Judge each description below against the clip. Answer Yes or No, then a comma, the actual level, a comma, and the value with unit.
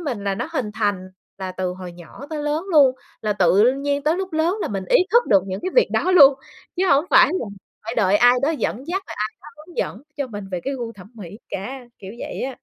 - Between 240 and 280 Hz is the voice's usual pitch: Yes, high, 245 Hz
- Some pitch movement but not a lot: No, wide, 7.3 semitones